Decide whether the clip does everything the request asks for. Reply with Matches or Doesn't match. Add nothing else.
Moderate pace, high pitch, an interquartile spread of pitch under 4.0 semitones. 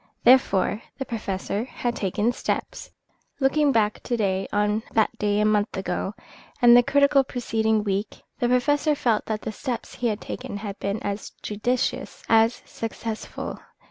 Matches